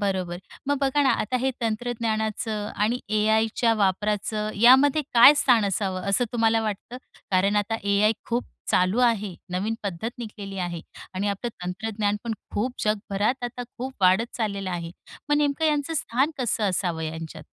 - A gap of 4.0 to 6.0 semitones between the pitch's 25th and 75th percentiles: No, average, 3.6 semitones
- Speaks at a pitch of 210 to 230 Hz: Yes, high, 215 Hz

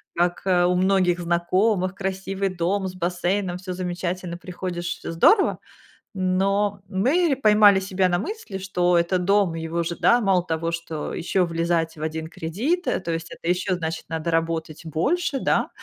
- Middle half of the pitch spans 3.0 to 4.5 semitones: No, narrow, 2.5 semitones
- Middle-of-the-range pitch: Yes, medium, 180 Hz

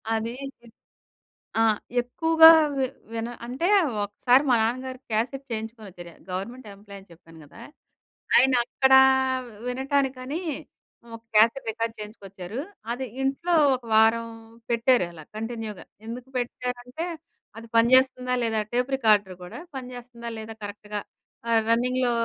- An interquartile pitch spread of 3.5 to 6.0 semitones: No, average, 2.8 semitones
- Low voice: No, high, 235 Hz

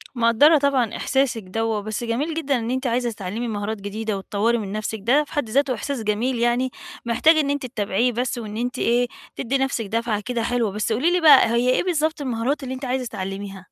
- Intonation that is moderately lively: Yes, average, 3.5 semitones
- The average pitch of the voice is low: No, high, 240 Hz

